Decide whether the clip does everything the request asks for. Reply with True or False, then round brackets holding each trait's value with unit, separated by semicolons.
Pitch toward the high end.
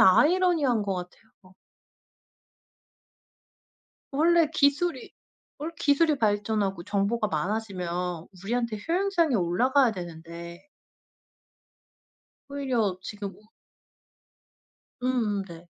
True (215 Hz)